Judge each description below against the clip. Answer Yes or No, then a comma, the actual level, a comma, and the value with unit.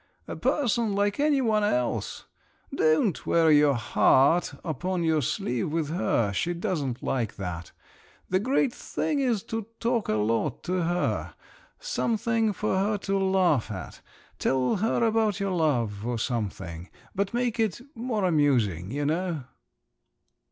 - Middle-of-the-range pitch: Yes, medium, 175 Hz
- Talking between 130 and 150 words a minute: Yes, average, 140 wpm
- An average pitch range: No, wide, 8.9 semitones